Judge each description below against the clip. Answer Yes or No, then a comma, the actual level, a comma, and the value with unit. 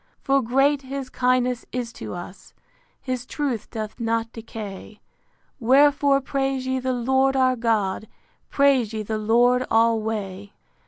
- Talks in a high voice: Yes, high, 245 Hz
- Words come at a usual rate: No, slow, 130 wpm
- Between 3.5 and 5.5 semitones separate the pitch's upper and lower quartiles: No, average, 3.1 semitones